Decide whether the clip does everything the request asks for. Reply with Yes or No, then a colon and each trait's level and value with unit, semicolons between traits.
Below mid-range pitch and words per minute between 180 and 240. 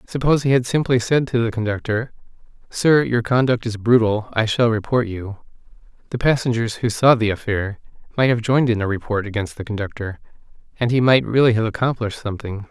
Yes: low, 115 Hz; average, 185 wpm